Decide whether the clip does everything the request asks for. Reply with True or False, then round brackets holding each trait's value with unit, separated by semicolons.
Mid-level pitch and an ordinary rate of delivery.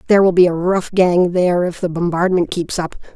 False (175 Hz; 230 wpm)